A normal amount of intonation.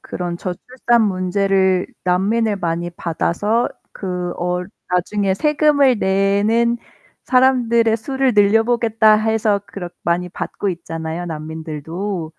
Yes: average, 4.2 semitones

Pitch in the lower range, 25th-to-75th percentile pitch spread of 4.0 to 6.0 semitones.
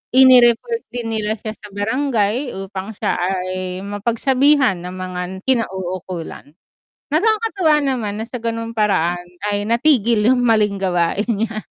No: high, 215 Hz; average, 4.9 semitones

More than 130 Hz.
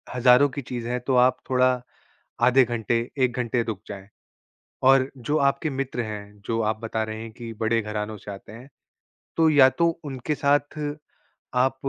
No: low, 125 Hz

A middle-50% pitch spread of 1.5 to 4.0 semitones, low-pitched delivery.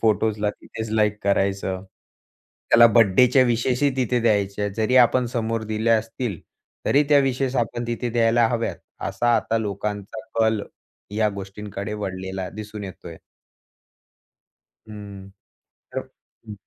Yes: average, 2.8 semitones; low, 110 Hz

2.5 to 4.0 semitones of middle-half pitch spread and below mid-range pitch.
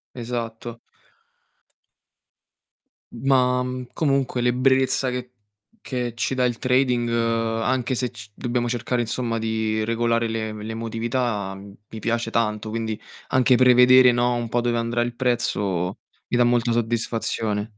No: narrow, 1.8 semitones; low, 120 Hz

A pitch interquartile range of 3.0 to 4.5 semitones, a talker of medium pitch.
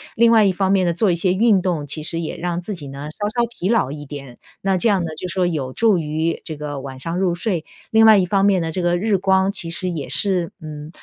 Yes: average, 4.0 semitones; medium, 175 Hz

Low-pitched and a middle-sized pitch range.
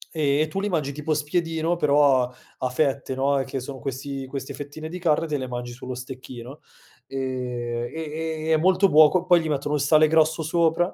No: medium, 145 Hz; average, 3.3 semitones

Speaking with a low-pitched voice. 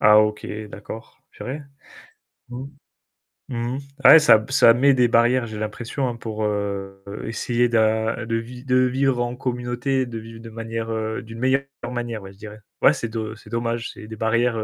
Yes: low, 115 Hz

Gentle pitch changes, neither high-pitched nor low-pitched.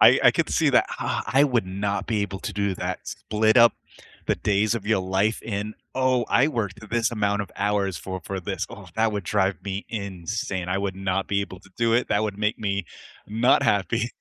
No: narrow, 2.3 semitones; low, 100 Hz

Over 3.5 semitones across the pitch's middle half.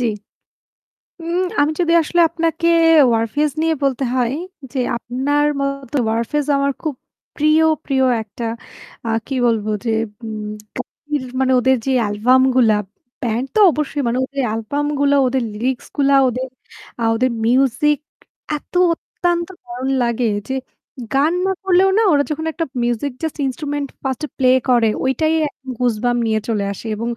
Yes: average, 4.0 semitones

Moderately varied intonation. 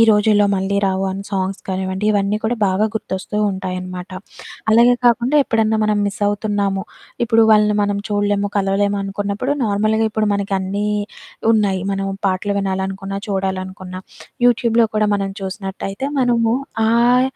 No: narrow, 2.0 semitones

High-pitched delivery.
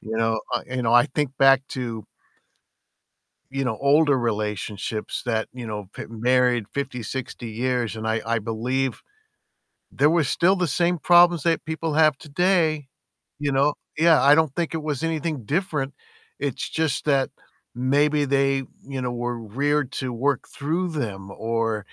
No: low, 135 Hz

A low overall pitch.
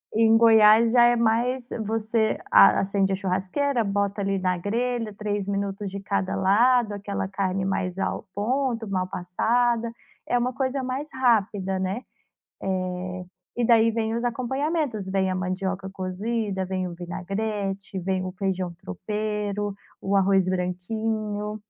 No: high, 205 Hz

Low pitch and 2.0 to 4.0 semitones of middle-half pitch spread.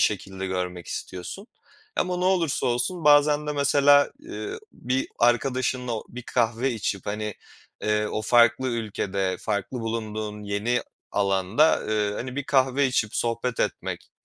No: low, 120 Hz; average, 4.5 semitones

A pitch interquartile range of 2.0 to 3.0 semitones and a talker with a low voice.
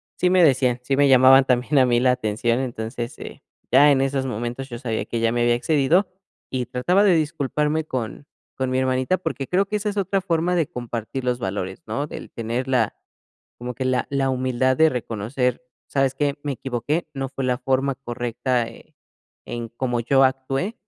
Yes: average, 2.7 semitones; low, 130 Hz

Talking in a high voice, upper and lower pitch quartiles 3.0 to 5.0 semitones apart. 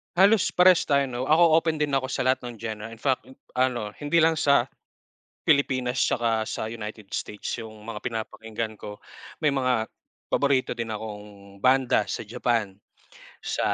No: low, 120 Hz; average, 4.2 semitones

